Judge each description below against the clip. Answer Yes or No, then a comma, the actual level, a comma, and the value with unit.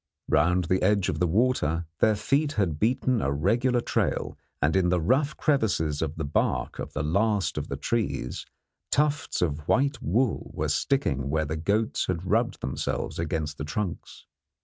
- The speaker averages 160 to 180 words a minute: Yes, average, 170 wpm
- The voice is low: Yes, very low, 90 Hz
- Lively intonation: Yes, wide, 7.2 semitones